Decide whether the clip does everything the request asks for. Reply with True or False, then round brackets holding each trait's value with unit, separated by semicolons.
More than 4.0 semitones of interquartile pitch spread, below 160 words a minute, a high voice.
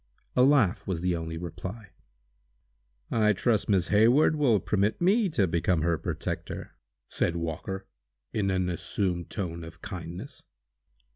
False (4.4 semitones; 135 wpm; 95 Hz)